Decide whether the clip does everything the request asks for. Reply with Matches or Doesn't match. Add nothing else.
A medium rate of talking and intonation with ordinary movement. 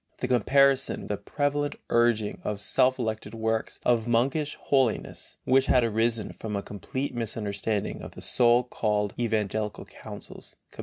Matches